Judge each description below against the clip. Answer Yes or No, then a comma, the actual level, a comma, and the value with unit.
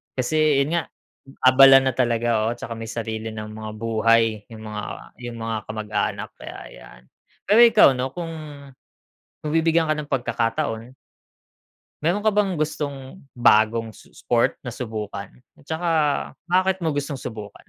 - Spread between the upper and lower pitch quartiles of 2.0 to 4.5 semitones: No, wide, 5.5 semitones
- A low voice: Yes, low, 120 Hz